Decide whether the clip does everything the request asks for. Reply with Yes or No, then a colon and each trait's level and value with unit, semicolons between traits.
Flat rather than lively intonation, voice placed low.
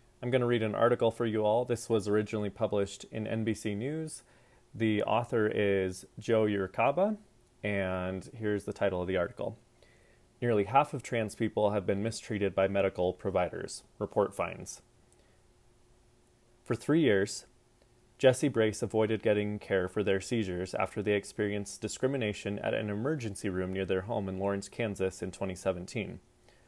No: average, 3.2 semitones; low, 110 Hz